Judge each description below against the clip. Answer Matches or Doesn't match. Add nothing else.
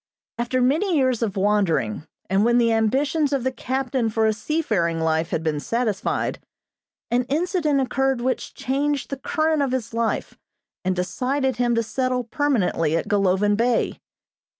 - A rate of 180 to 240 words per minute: Doesn't match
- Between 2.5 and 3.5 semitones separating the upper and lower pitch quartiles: Doesn't match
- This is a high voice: Matches